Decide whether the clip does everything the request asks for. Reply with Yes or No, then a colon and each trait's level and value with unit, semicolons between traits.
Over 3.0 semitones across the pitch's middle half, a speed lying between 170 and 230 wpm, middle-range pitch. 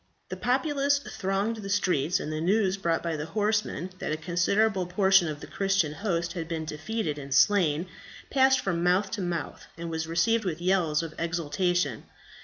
Yes: average, 3.9 semitones; average, 180 wpm; medium, 180 Hz